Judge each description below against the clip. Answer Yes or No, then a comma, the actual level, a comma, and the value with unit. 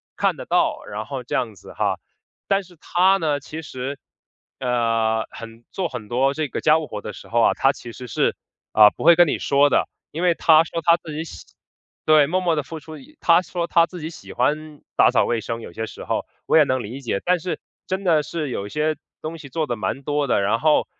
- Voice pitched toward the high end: No, medium, 150 Hz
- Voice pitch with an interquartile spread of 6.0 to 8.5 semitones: No, wide, 5.5 semitones